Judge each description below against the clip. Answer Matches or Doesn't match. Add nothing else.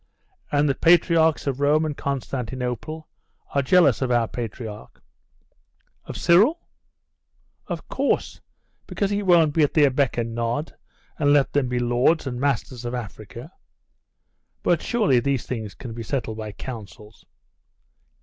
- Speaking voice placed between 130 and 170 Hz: Matches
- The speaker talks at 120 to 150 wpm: Matches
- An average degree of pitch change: Matches